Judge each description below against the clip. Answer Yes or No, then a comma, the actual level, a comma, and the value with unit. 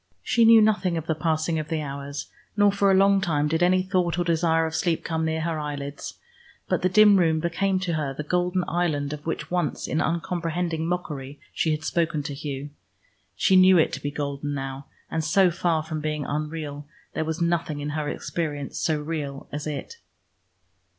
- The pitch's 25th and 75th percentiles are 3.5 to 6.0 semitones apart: No, average, 3.1 semitones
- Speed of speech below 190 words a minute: No, average, 195 wpm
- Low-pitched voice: No, medium, 160 Hz